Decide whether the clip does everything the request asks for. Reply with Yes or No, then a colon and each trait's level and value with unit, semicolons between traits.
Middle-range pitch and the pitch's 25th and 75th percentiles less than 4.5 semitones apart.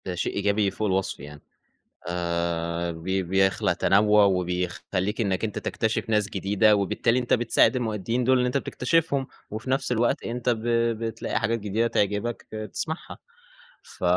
No: low, 105 Hz; average, 3.8 semitones